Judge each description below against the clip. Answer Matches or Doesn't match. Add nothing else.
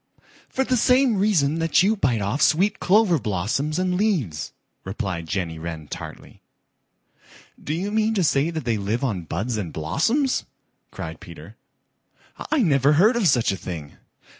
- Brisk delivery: Doesn't match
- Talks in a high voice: Doesn't match